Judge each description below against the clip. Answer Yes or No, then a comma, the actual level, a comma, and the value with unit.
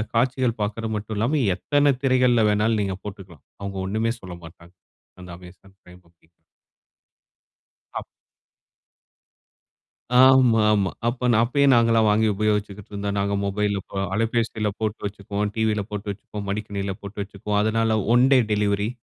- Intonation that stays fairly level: Yes, narrow, 2.3 semitones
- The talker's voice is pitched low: Yes, low, 105 Hz